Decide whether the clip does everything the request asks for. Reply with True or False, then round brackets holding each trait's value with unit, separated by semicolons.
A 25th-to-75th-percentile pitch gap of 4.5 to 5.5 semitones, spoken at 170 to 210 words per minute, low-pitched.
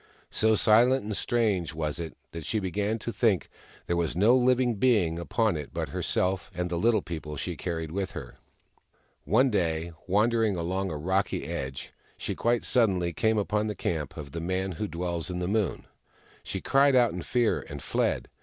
True (4.8 semitones; 185 wpm; 95 Hz)